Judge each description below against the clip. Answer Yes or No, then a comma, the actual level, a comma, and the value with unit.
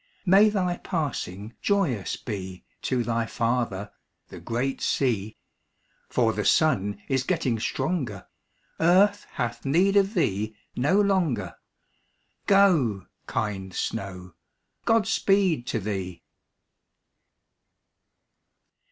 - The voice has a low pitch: Yes, low, 125 Hz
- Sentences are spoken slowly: Yes, slow, 100 wpm